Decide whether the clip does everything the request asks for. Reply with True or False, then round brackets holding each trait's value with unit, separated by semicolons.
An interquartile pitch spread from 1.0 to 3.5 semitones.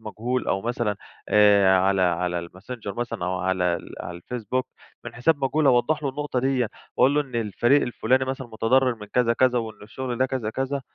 False (4.3 semitones)